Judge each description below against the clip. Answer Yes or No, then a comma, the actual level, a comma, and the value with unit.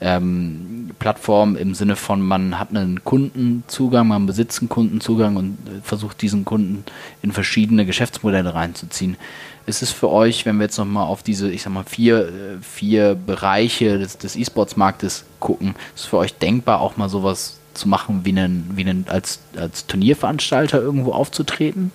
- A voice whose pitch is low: Yes, low, 105 Hz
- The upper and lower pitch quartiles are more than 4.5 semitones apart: No, average, 2.9 semitones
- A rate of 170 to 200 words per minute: No, average, 160 wpm